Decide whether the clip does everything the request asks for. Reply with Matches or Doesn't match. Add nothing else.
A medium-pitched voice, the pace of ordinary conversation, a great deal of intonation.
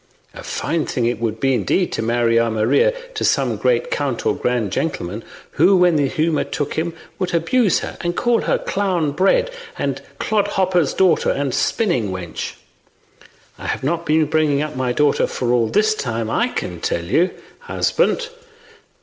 Matches